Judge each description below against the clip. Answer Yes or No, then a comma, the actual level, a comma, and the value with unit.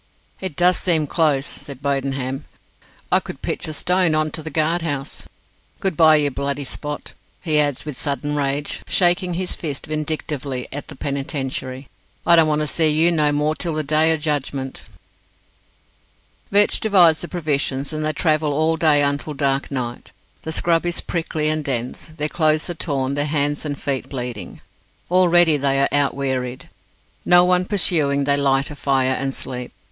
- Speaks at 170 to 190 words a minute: Yes, average, 175 wpm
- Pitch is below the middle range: No, medium, 150 Hz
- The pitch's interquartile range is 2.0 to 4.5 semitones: Yes, narrow, 2.6 semitones